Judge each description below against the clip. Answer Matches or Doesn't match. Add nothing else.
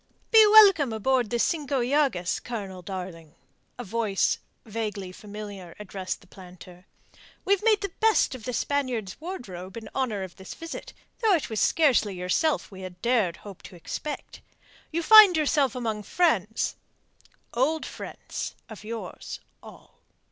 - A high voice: Matches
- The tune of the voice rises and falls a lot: Matches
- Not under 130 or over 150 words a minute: Matches